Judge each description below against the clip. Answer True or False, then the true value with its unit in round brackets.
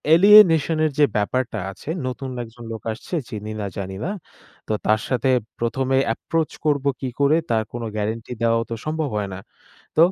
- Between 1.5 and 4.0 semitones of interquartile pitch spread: False (5.5 semitones)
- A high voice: False (125 Hz)